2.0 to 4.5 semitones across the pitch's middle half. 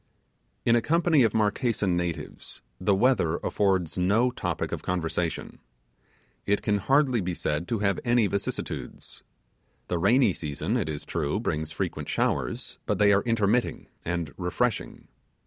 No: average, 5.1 semitones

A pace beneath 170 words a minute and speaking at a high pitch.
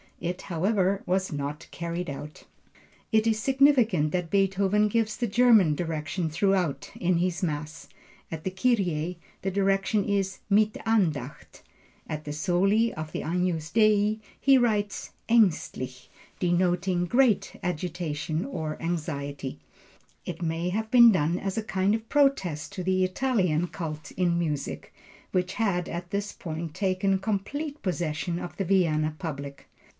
No: average, 140 wpm; medium, 180 Hz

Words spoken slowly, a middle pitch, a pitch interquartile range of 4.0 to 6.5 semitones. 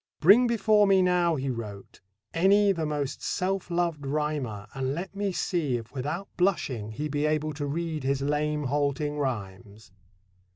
No: average, 160 wpm; medium, 150 Hz; average, 4.8 semitones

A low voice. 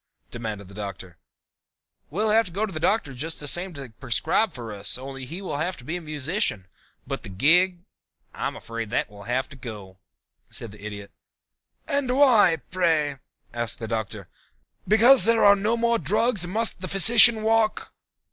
No: medium, 155 Hz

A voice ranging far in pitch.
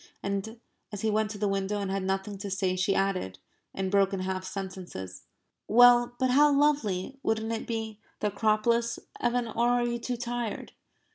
No: average, 3.6 semitones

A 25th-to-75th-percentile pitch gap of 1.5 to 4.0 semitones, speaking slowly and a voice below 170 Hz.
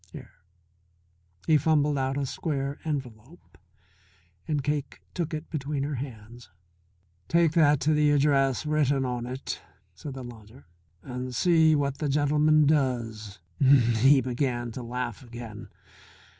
Yes: average, 3.5 semitones; slow, 130 wpm; low, 135 Hz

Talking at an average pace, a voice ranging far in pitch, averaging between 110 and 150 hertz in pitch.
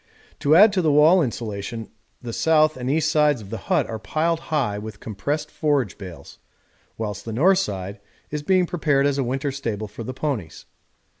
Yes: average, 190 wpm; wide, 5.9 semitones; low, 135 Hz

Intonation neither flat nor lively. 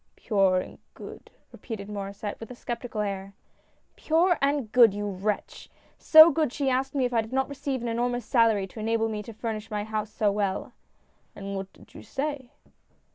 Yes: average, 4.0 semitones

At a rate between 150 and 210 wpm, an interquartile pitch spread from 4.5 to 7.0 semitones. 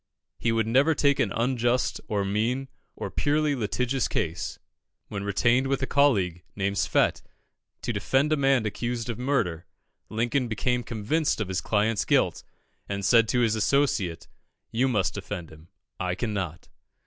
Yes: average, 160 wpm; average, 4.8 semitones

